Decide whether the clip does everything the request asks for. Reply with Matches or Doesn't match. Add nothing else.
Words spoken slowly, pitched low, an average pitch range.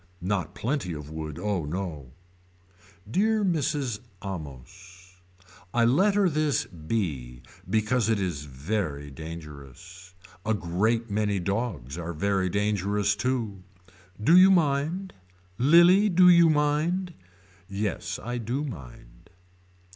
Doesn't match